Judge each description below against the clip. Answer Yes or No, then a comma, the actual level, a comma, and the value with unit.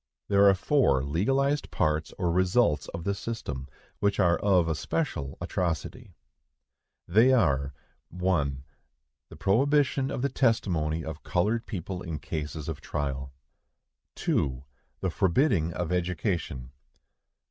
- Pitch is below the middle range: Yes, very low, 90 Hz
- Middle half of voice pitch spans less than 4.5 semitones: No, wide, 5.4 semitones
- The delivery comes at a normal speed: No, slow, 120 wpm